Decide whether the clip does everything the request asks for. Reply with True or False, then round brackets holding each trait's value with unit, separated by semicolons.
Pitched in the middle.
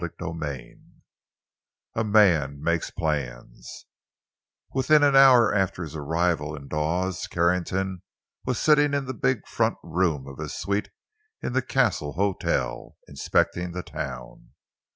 False (90 Hz)